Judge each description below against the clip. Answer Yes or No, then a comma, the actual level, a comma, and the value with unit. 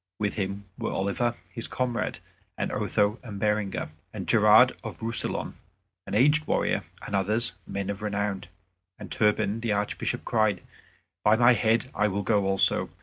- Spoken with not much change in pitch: Yes, narrow, 2.3 semitones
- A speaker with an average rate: Yes, average, 155 wpm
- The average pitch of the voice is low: Yes, low, 105 Hz